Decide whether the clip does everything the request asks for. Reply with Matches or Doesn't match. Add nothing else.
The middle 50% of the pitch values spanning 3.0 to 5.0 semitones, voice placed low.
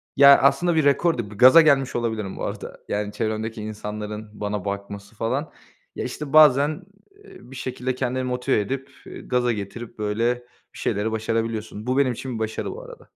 Matches